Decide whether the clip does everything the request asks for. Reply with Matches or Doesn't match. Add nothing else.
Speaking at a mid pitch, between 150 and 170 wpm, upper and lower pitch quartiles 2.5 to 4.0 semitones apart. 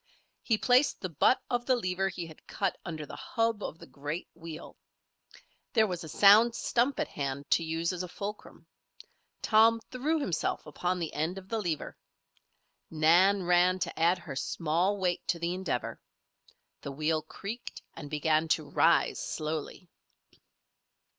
Doesn't match